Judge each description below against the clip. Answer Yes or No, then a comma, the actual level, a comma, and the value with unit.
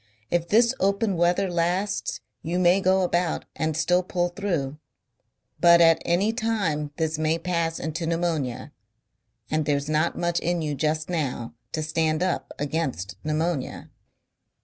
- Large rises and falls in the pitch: No, narrow, 2.4 semitones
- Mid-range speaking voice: Yes, medium, 170 Hz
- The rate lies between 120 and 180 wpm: Yes, average, 145 wpm